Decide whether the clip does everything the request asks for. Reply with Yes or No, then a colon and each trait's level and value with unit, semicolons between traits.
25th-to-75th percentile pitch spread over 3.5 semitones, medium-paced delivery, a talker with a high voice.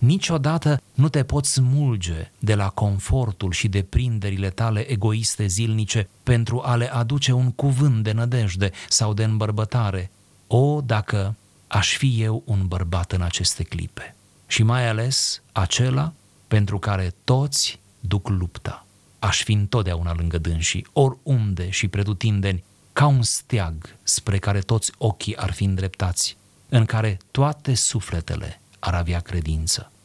No: average, 3.9 semitones; average, 140 wpm; low, 110 Hz